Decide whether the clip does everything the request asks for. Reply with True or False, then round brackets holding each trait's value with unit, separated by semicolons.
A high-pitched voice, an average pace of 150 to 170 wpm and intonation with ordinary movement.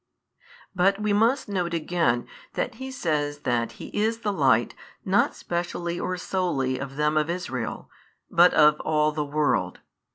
False (170 Hz; 160 wpm; 4.7 semitones)